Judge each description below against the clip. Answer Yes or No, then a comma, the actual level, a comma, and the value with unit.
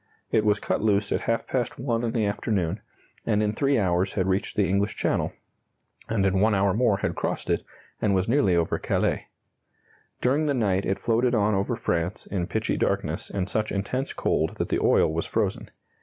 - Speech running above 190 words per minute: Yes, average, 200 wpm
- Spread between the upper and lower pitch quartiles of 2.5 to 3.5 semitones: Yes, average, 3.0 semitones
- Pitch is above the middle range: No, low, 105 Hz